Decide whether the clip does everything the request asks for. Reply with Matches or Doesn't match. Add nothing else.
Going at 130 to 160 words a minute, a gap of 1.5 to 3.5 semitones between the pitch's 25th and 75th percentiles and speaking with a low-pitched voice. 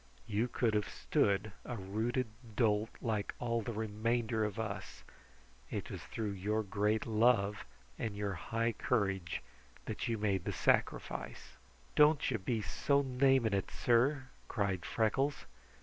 Matches